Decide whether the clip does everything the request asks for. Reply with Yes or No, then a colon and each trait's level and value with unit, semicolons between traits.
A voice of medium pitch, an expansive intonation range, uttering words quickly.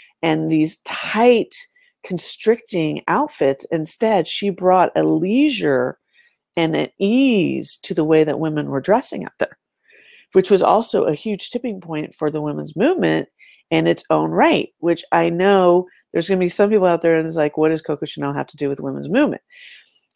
No: medium, 175 Hz; wide, 6.3 semitones; average, 180 wpm